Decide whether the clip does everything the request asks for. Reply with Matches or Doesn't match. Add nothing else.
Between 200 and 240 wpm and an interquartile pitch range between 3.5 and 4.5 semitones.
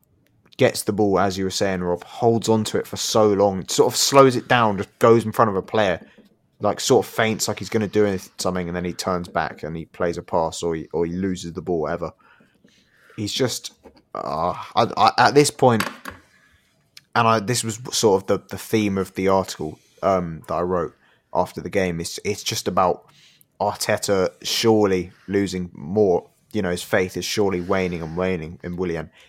Matches